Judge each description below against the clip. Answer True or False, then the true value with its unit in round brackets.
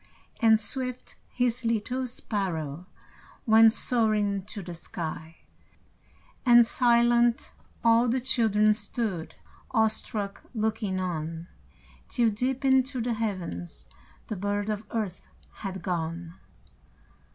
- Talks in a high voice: True (215 Hz)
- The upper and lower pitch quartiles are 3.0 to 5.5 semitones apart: True (4.1 semitones)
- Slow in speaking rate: True (105 wpm)